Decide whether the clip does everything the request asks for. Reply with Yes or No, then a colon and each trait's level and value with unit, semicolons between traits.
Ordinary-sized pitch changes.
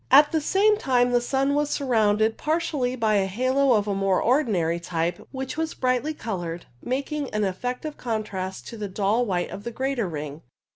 No: wide, 5.8 semitones